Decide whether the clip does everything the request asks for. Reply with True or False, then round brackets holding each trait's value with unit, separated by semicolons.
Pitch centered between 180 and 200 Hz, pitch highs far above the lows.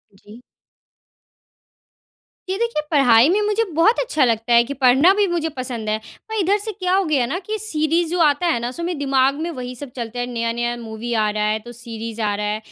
False (260 Hz; 7.0 semitones)